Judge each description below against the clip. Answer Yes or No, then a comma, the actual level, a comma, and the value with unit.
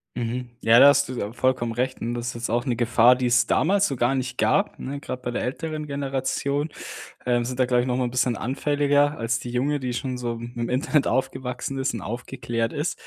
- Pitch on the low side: Yes, low, 125 Hz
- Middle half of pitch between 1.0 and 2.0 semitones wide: No, narrow, 2.4 semitones